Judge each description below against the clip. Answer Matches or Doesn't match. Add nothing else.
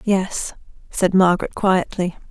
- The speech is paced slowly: Matches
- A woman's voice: Matches